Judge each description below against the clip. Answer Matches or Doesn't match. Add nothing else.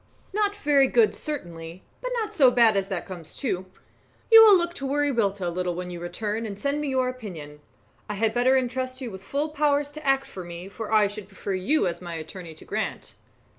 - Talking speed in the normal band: Doesn't match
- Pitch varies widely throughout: Matches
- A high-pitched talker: Matches